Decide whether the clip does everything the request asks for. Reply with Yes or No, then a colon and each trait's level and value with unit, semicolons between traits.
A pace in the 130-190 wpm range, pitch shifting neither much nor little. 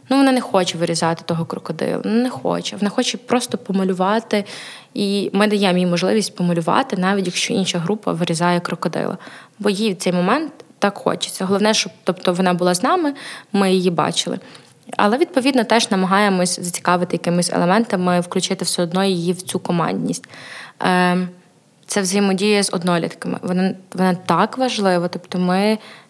Yes: average, 150 wpm; average, 3.1 semitones